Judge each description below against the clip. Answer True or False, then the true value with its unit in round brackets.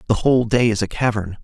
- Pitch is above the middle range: False (110 Hz)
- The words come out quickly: True (250 wpm)